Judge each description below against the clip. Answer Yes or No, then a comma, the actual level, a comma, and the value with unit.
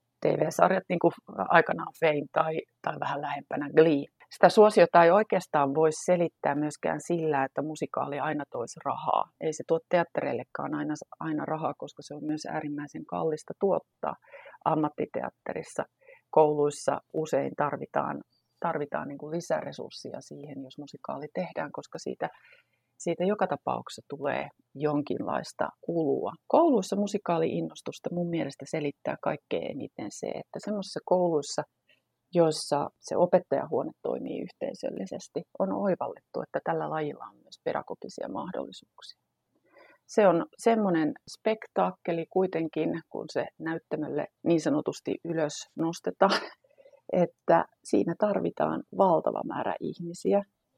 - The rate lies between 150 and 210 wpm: No, average, 115 wpm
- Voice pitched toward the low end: No, medium, 160 Hz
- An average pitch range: Yes, average, 3.6 semitones